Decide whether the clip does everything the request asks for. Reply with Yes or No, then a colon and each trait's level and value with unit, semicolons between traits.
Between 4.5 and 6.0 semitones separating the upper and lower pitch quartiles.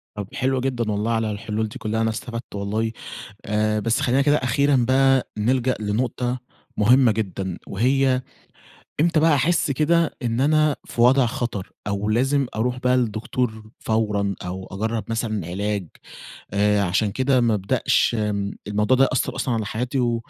No: average, 3.6 semitones